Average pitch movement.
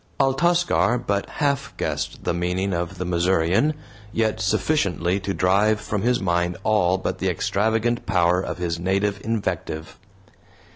Yes: average, 4.0 semitones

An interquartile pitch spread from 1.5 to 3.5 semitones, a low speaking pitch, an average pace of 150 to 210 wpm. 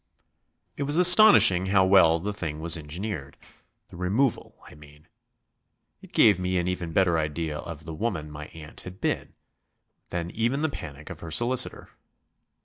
No: average, 4.9 semitones; very low, 90 Hz; average, 160 wpm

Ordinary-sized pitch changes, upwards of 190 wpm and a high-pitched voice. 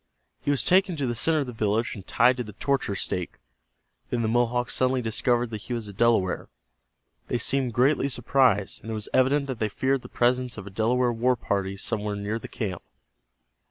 No: average, 3.2 semitones; fast, 205 wpm; low, 120 Hz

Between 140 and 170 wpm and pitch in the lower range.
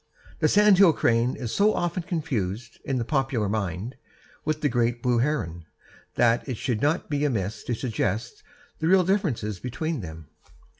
Yes: average, 160 wpm; low, 125 Hz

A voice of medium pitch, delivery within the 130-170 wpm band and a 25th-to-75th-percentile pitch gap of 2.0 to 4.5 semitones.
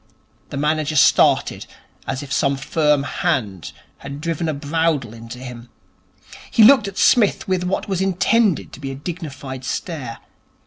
No: medium, 150 Hz; average, 150 wpm; average, 4.9 semitones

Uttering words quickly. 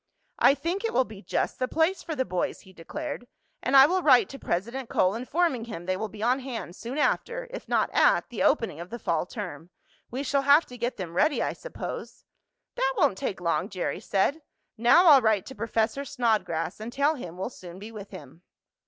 Yes: fast, 215 wpm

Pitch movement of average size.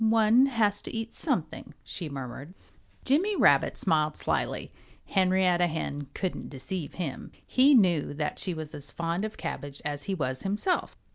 No: wide, 6.4 semitones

